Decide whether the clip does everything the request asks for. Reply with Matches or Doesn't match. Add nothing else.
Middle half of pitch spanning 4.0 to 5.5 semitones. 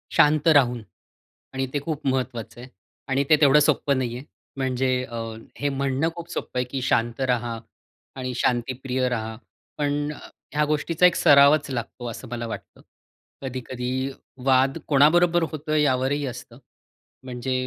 Doesn't match